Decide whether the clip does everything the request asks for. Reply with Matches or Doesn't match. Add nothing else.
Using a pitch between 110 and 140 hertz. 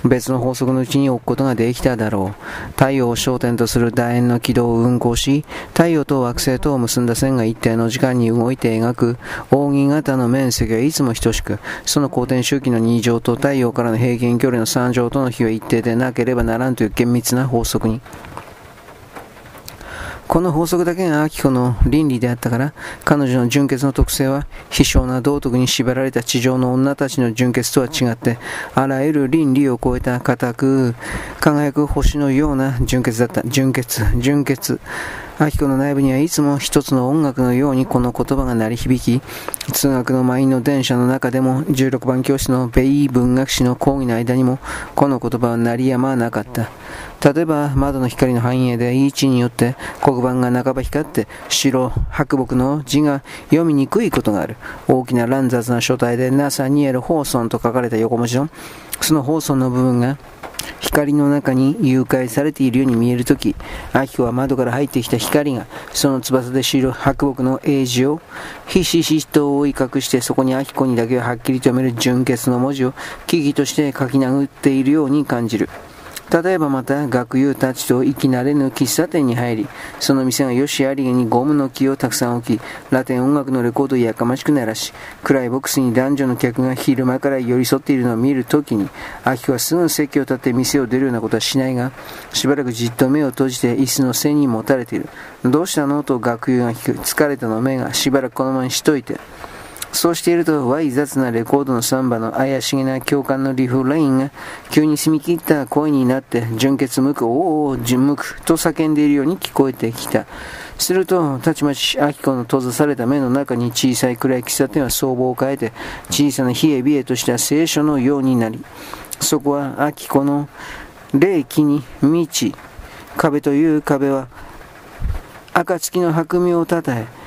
Matches